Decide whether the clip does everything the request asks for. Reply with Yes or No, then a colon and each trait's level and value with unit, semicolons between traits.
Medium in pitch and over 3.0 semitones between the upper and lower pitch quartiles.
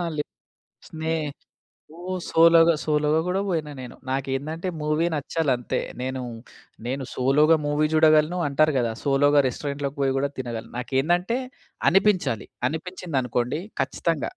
Yes: medium, 150 Hz; average, 3.4 semitones